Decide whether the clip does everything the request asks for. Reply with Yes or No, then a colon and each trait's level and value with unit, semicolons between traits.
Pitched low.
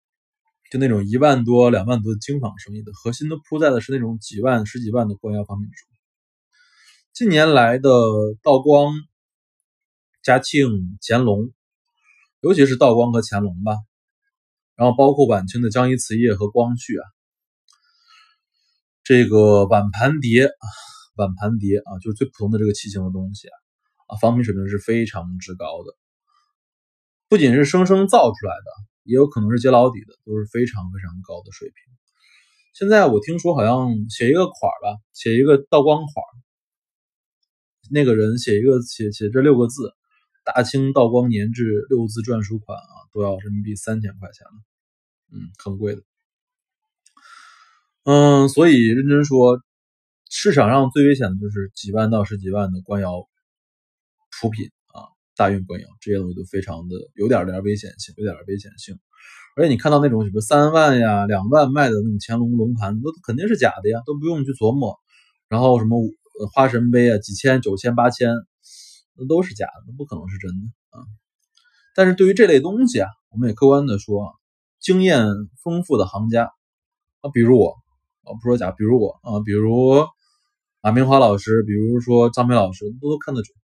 Yes: low, 120 Hz